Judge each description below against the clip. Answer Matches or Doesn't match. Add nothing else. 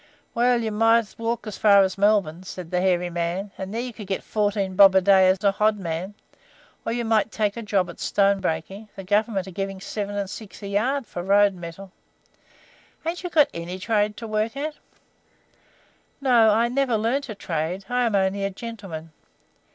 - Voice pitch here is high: Matches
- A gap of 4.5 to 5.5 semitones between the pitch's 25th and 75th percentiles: Doesn't match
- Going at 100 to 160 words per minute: Doesn't match